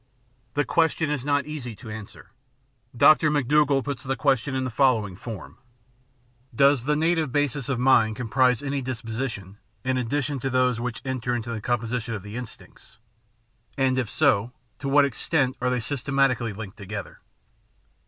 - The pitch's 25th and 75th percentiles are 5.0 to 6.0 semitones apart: No, average, 3.5 semitones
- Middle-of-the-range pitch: No, low, 130 Hz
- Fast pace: No, average, 165 wpm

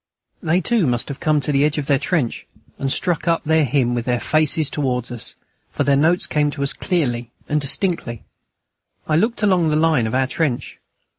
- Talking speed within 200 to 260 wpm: Yes, fast, 205 wpm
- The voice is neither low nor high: Yes, medium, 150 Hz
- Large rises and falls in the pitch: No, average, 3.9 semitones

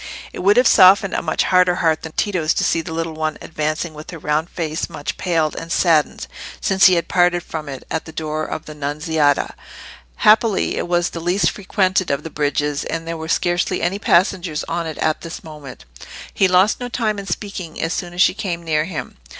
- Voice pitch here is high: No, medium, 165 Hz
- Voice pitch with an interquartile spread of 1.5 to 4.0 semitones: Yes, average, 2.9 semitones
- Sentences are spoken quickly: Yes, fast, 215 wpm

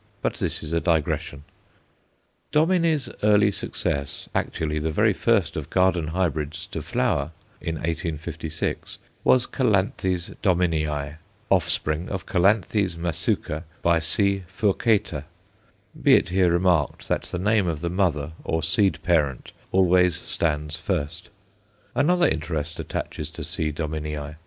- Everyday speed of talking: No, slow, 125 wpm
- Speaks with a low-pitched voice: Yes, very low, 85 Hz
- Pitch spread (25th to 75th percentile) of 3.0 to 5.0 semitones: Yes, average, 3.9 semitones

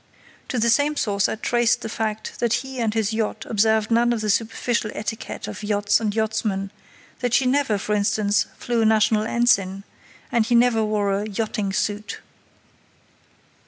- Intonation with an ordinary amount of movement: No, narrow, 2.0 semitones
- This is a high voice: Yes, high, 220 Hz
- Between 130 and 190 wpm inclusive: Yes, average, 170 wpm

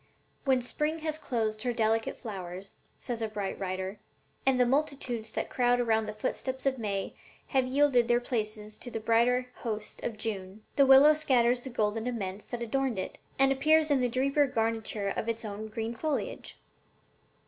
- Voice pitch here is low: No, high, 235 Hz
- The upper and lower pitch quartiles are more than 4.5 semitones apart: No, average, 3.5 semitones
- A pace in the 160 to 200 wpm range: Yes, average, 175 wpm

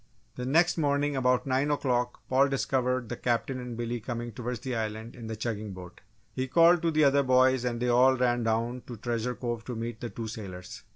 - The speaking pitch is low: Yes, low, 125 Hz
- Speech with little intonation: Yes, narrow, 2.2 semitones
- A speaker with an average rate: No, fast, 215 wpm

